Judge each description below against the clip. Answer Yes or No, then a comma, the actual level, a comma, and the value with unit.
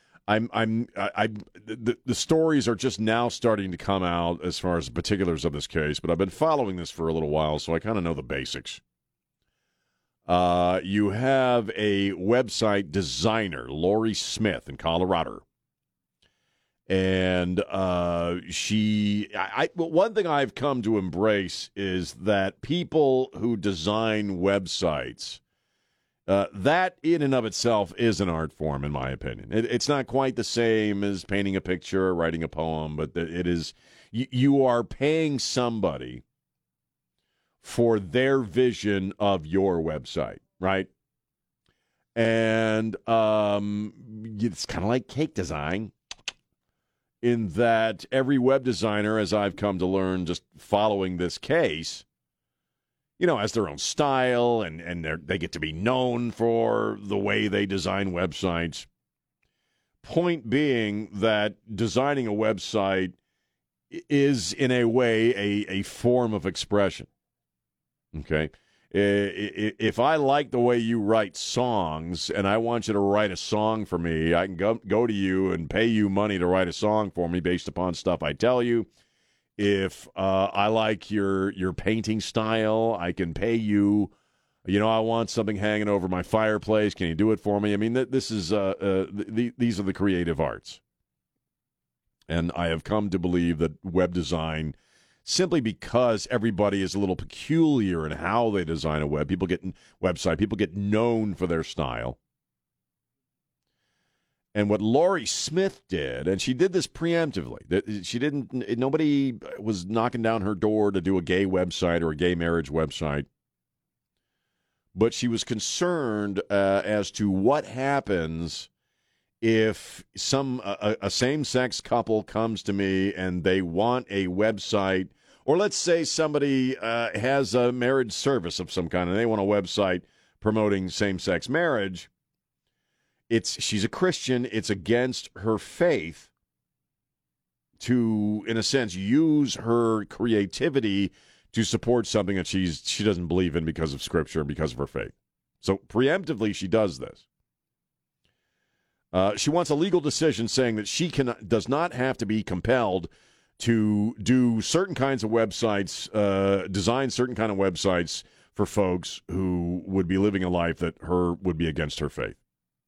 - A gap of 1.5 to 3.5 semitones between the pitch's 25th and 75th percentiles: No, average, 4.2 semitones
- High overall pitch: No, low, 105 Hz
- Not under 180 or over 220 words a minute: No, average, 160 wpm